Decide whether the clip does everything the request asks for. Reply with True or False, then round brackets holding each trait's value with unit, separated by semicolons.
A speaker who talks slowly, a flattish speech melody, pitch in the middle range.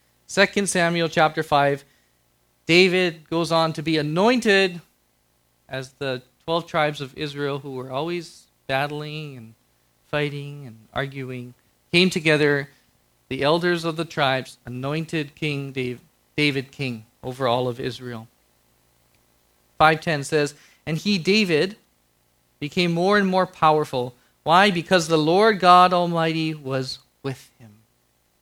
False (120 wpm; 5.4 semitones; 145 Hz)